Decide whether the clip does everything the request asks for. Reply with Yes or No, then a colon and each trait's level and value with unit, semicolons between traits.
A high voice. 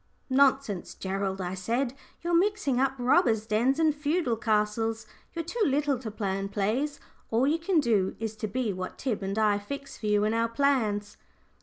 Yes: high, 230 Hz